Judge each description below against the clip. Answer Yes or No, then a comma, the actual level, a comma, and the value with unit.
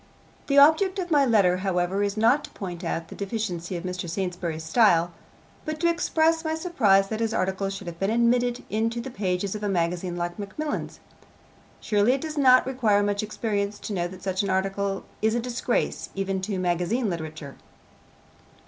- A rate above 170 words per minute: Yes, average, 185 wpm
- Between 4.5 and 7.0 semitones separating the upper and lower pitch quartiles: Yes, average, 4.8 semitones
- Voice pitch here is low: No, high, 200 Hz